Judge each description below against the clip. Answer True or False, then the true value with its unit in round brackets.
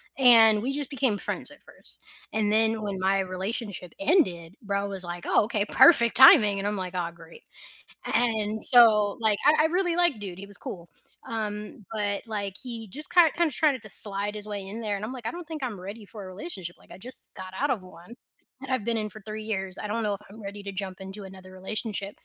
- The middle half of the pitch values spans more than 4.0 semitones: False (3.2 semitones)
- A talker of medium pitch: False (210 Hz)